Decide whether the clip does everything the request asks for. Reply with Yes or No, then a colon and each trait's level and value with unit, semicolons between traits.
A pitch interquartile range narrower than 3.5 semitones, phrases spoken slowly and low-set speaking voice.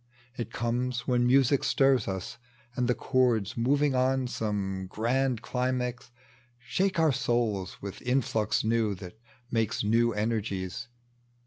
Yes: average, 2.9 semitones; slow, 125 wpm; low, 120 Hz